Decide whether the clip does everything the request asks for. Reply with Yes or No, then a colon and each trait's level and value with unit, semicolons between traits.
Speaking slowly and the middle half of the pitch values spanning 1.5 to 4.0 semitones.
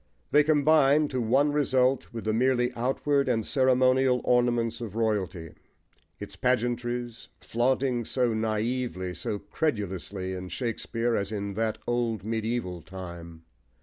Yes: slow, 125 wpm; average, 3.4 semitones